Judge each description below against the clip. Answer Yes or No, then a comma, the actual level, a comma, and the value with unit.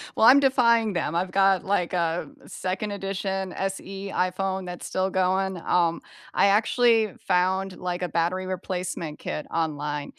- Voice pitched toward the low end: No, medium, 185 Hz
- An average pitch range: No, narrow, 1.6 semitones